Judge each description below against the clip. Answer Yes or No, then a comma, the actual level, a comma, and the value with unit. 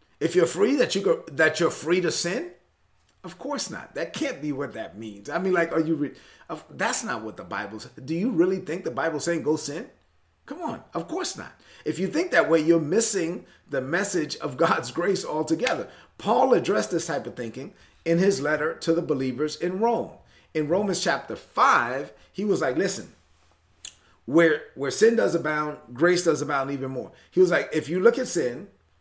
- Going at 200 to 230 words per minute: Yes, fast, 205 wpm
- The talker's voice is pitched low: No, medium, 160 Hz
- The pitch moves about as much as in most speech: Yes, average, 4.7 semitones